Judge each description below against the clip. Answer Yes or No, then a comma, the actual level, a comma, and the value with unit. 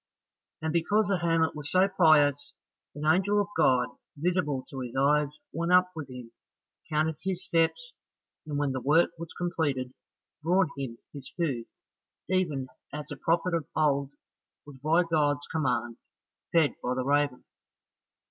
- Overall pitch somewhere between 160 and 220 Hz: No, medium, 150 Hz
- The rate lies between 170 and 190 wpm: No, average, 150 wpm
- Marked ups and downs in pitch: No, average, 3.5 semitones